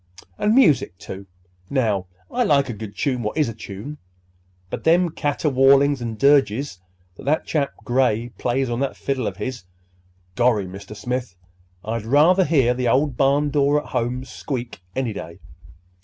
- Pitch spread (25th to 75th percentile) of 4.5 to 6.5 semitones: Yes, average, 4.8 semitones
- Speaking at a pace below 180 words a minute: Yes, average, 155 wpm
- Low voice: Yes, low, 125 Hz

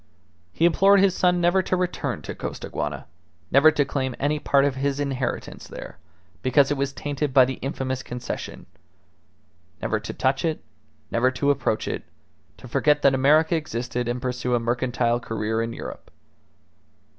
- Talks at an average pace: Yes, average, 160 wpm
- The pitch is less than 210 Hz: Yes, low, 135 Hz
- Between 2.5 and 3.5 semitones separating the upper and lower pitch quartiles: Yes, average, 3.2 semitones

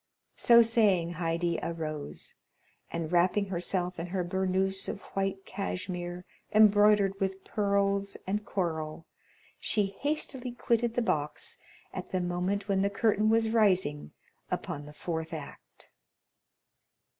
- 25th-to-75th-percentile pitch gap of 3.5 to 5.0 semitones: No, average, 3.1 semitones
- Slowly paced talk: Yes, slow, 120 wpm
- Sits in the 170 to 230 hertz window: Yes, high, 190 Hz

